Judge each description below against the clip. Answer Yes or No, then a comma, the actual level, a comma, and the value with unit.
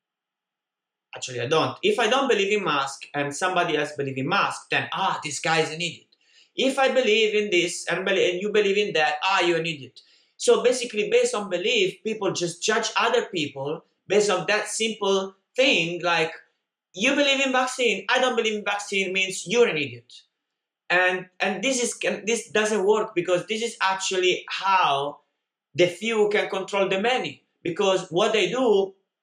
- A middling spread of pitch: Yes, average, 4.8 semitones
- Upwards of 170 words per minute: Yes, average, 180 wpm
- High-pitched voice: Yes, high, 195 Hz